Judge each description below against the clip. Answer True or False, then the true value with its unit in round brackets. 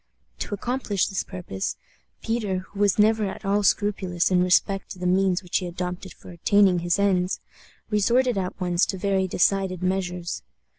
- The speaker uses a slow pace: False (165 wpm)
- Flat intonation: True (2.1 semitones)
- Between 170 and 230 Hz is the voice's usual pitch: True (190 Hz)